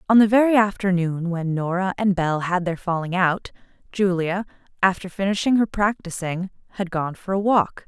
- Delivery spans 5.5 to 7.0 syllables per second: No, 5.1 syllables/s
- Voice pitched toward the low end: No, medium, 185 Hz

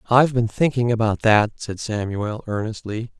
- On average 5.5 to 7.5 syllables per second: No, 4.7 syllables/s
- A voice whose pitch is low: Yes, low, 110 Hz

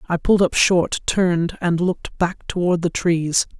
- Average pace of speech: Yes, average, 185 wpm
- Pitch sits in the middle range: Yes, medium, 175 Hz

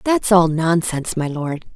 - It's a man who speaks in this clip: No, female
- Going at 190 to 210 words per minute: No, average, 170 wpm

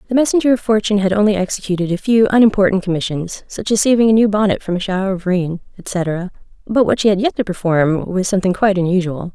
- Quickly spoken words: Yes, fast, 220 wpm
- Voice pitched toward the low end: No, high, 195 Hz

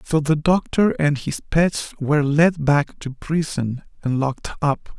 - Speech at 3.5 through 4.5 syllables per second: Yes, 4.0 syllables/s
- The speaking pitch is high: No, medium, 150 Hz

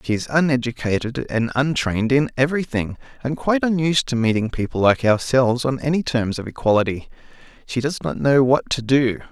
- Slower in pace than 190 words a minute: Yes, average, 175 wpm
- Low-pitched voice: Yes, low, 130 Hz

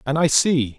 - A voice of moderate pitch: Yes, medium, 145 Hz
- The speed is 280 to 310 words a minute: No, fast, 230 wpm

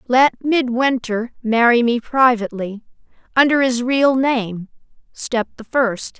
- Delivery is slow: Yes, slow, 105 wpm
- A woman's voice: Yes, female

